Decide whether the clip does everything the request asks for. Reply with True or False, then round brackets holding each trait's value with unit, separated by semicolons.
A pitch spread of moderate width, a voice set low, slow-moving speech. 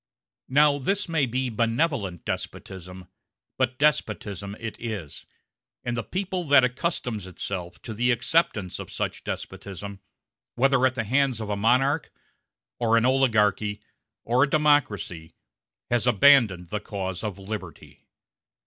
True (5.0 semitones; 115 Hz; 130 wpm)